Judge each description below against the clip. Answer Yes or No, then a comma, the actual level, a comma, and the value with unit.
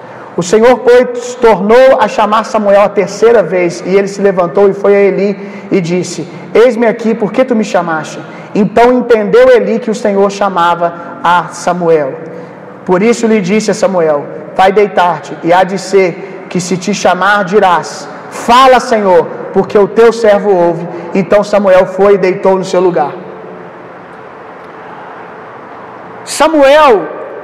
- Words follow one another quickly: Yes, fast, 155 wpm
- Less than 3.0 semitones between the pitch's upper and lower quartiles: No, average, 4.1 semitones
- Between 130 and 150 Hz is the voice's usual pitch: No, high, 200 Hz